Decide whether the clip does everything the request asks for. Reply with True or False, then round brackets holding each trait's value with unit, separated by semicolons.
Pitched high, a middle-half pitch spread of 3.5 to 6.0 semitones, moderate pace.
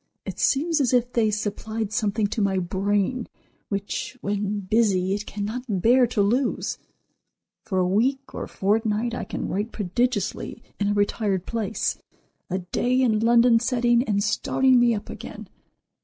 False (215 Hz; 3.0 semitones; 155 wpm)